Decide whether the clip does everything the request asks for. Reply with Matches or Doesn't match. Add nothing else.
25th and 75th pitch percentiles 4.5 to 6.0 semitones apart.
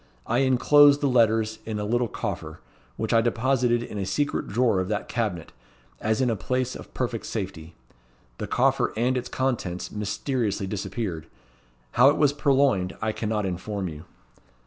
Doesn't match